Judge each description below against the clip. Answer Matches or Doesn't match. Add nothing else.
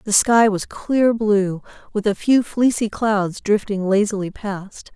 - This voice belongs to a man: Doesn't match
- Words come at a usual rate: Matches